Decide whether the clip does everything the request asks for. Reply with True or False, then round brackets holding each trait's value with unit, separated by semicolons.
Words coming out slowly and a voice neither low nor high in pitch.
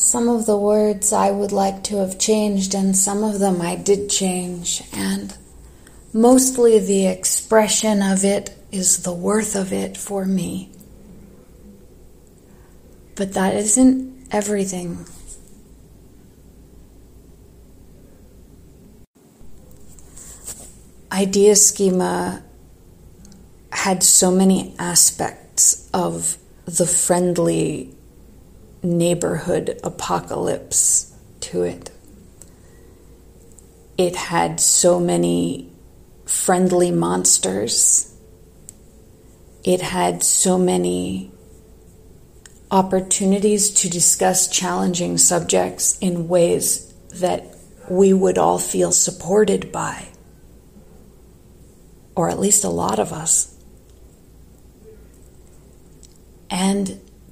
True (85 wpm; 180 Hz)